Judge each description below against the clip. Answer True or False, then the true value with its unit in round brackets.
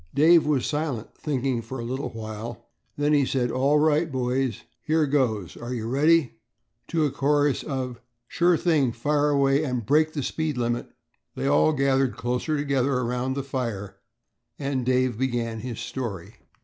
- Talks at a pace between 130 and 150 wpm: False (160 wpm)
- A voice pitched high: False (130 Hz)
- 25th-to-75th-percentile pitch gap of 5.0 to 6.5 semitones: False (3.5 semitones)